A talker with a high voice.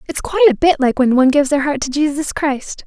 Yes: very high, 285 Hz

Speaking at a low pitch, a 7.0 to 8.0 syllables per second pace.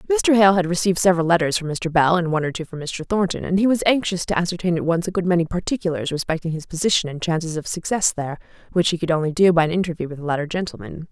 No: medium, 170 Hz; 7.2 syllables/s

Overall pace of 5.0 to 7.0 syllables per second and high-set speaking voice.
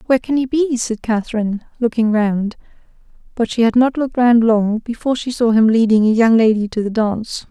Yes: 5.8 syllables/s; high, 230 Hz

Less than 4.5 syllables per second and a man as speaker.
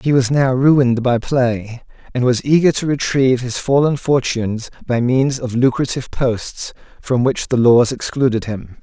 No: 4.6 syllables/s; male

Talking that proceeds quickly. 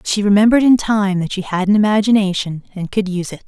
Yes: fast, 240 wpm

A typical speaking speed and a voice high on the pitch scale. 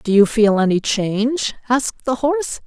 Yes: average, 180 wpm; high, 235 Hz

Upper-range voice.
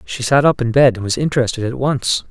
No: low, 125 Hz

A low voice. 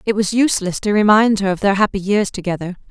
No: high, 200 Hz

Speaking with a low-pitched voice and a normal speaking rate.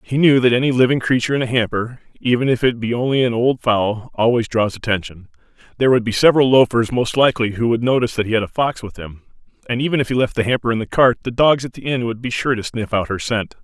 No: low, 120 Hz; fast, 265 wpm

